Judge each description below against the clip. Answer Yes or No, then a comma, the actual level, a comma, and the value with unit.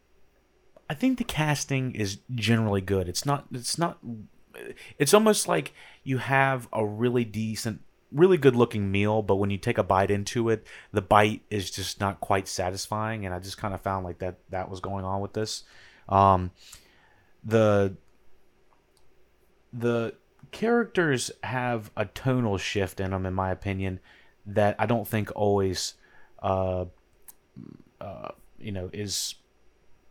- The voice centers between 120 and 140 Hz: No, low, 105 Hz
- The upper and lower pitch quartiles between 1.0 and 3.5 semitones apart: No, average, 3.9 semitones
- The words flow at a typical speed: Yes, average, 145 wpm